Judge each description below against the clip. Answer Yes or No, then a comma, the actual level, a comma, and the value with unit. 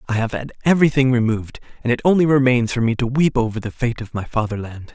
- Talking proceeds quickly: Yes, fast, 230 wpm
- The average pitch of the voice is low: Yes, low, 120 Hz